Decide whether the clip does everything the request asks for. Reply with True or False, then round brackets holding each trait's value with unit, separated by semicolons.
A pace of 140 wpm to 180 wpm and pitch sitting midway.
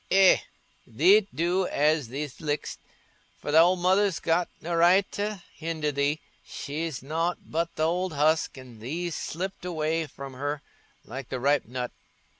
True (155 wpm; 160 Hz)